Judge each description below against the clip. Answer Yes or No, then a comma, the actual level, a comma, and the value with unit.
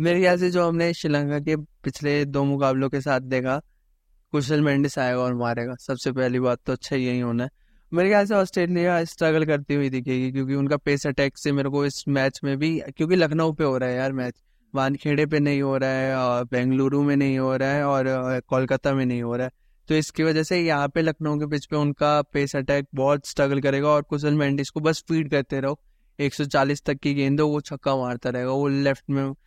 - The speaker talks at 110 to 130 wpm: No, average, 155 wpm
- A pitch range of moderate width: No, narrow, 2.1 semitones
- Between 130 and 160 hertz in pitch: Yes, medium, 140 Hz